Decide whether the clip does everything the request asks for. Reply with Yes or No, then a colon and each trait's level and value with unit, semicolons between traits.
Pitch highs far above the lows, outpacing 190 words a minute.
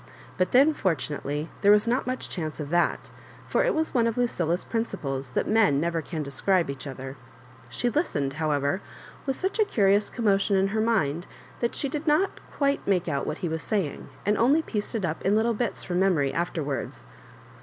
Yes: wide, 7.1 semitones; average, 200 wpm